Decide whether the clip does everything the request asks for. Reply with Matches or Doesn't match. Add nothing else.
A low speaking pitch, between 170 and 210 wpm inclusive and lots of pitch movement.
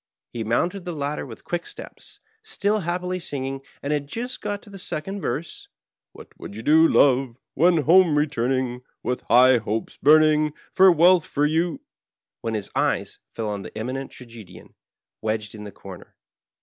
Doesn't match